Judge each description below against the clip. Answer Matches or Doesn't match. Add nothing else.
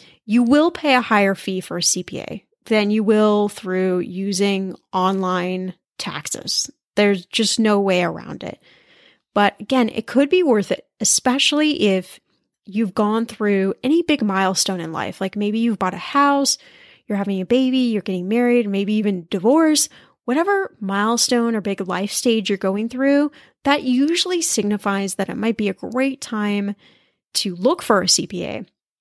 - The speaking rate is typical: Matches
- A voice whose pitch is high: Matches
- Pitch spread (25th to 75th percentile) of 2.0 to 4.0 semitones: Doesn't match